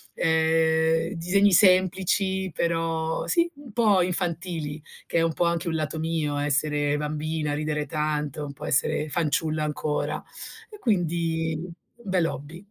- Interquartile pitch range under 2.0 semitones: No, average, 2.7 semitones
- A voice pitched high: No, medium, 160 Hz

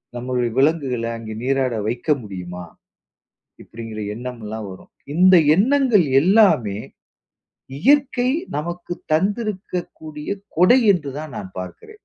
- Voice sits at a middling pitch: Yes, medium, 150 Hz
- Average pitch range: No, wide, 8.2 semitones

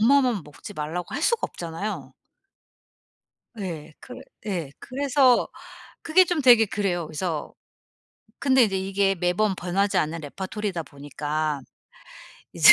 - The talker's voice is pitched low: No, high, 190 Hz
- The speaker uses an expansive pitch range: Yes, wide, 6.6 semitones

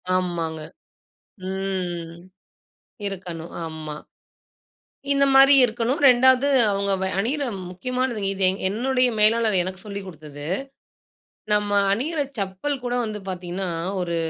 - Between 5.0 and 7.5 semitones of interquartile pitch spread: Yes, wide, 5.5 semitones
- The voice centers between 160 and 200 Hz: Yes, high, 195 Hz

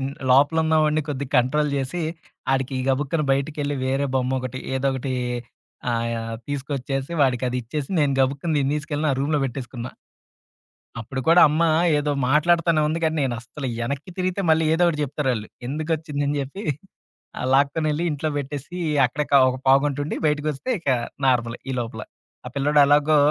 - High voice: No, medium, 140 Hz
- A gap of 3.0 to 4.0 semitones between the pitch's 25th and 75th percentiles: No, narrow, 2.6 semitones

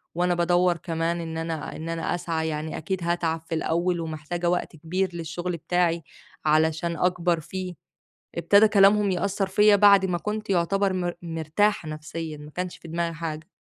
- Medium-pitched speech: Yes, medium, 170 Hz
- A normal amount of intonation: No, narrow, 2.2 semitones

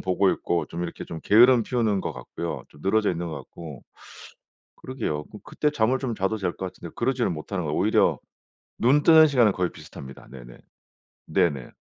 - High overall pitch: No, very low, 95 Hz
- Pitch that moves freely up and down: Yes, wide, 6.5 semitones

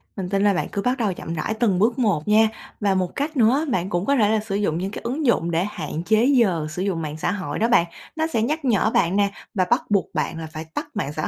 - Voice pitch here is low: No, high, 200 Hz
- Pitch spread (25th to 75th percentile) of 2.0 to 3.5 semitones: No, average, 4.8 semitones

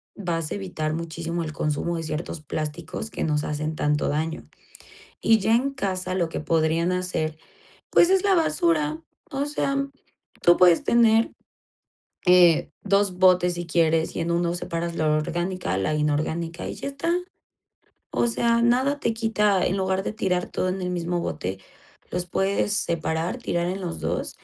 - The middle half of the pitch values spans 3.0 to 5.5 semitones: Yes, average, 3.6 semitones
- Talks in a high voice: No, medium, 175 Hz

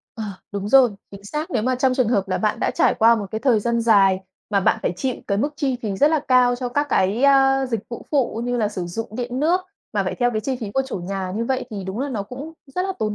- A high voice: Yes, high, 235 Hz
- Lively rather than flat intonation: No, average, 4.5 semitones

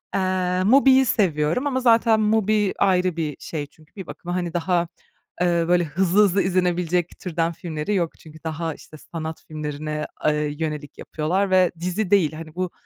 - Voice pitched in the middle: Yes, medium, 175 Hz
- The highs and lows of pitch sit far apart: No, average, 3.4 semitones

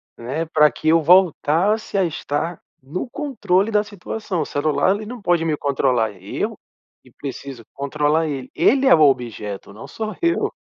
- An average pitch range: No, wide, 6.5 semitones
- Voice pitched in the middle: Yes, medium, 160 Hz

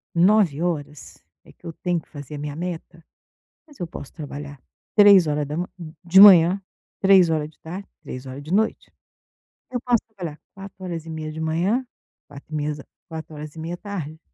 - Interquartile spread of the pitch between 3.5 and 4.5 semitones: Yes, average, 3.9 semitones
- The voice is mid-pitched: Yes, medium, 165 Hz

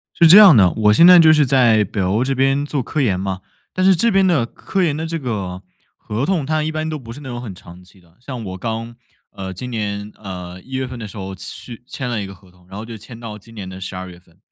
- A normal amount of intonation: No, wide, 6.8 semitones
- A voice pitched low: Yes, low, 115 Hz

